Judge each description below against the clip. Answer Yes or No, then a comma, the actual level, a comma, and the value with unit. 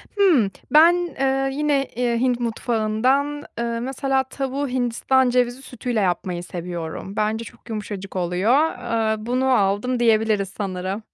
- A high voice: Yes, high, 240 Hz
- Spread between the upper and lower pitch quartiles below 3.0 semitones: No, average, 4.0 semitones